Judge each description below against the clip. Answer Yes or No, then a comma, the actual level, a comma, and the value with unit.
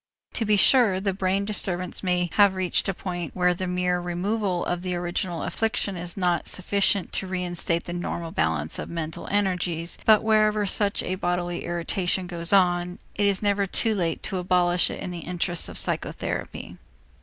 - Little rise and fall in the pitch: Yes, narrow, 2.1 semitones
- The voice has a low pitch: No, medium, 180 Hz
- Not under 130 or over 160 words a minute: No, average, 180 wpm